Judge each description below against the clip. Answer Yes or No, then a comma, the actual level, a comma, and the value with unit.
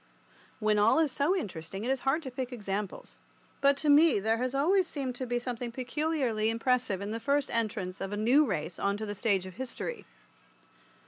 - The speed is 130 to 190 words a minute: No, average, 200 wpm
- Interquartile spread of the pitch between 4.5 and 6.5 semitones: Yes, average, 5.0 semitones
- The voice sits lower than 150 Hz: No, high, 245 Hz